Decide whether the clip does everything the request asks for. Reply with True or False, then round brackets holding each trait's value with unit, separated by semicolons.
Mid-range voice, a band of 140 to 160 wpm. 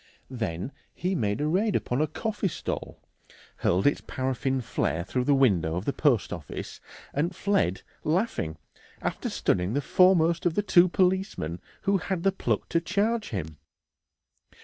True (150 Hz; 155 wpm)